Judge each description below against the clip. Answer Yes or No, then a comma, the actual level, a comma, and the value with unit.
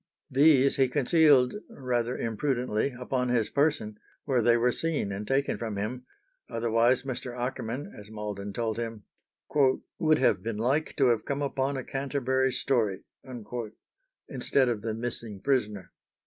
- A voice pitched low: Yes, low, 125 Hz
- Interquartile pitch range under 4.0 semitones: Yes, average, 3.4 semitones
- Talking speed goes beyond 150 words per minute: No, average, 145 wpm